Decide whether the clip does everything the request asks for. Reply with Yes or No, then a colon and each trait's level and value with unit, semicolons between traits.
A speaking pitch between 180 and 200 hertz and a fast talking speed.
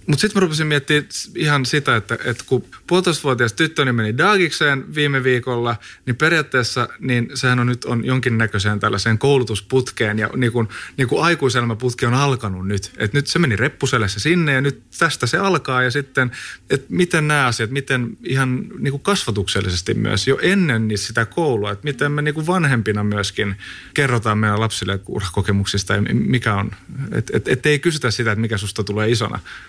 No: low, 125 Hz; fast, 170 wpm